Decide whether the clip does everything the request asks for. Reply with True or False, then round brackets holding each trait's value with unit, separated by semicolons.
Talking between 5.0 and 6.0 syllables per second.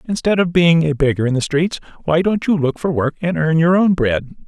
True (5.6 syllables/s)